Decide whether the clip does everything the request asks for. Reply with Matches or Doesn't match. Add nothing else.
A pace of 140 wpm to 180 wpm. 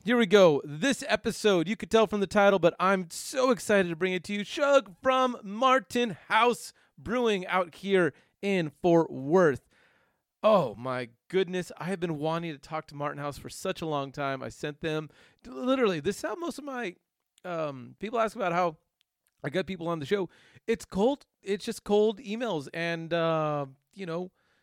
Doesn't match